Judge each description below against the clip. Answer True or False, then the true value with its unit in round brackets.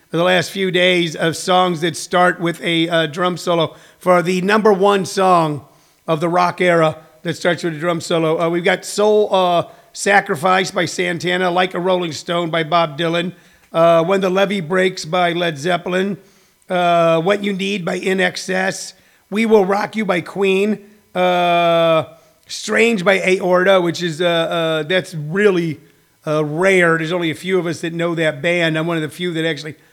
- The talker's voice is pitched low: False (175 Hz)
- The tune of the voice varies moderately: False (2.2 semitones)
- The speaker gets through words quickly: False (185 wpm)